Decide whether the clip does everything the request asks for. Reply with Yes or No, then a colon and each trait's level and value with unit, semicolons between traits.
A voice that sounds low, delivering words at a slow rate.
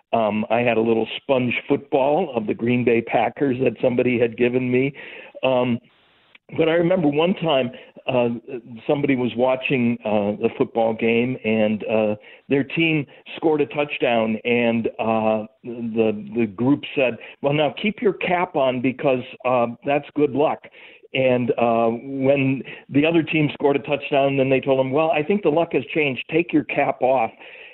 No: low, 130 Hz; average, 175 wpm